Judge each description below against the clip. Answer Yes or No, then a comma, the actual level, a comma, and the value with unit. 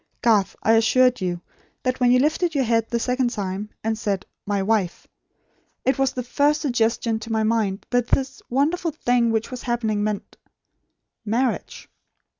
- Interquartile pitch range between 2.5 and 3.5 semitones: Yes, average, 2.9 semitones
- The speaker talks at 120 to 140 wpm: No, average, 165 wpm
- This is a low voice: No, high, 230 Hz